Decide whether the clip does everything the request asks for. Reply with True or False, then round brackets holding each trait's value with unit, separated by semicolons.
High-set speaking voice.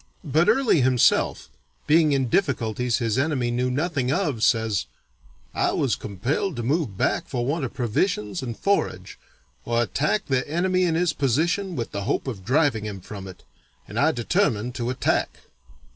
False (130 Hz)